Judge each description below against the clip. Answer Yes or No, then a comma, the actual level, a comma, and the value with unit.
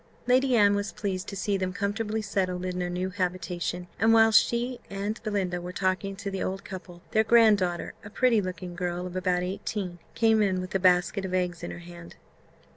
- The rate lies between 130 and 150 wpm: No, fast, 205 wpm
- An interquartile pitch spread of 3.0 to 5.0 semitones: No, narrow, 2.6 semitones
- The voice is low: No, high, 190 Hz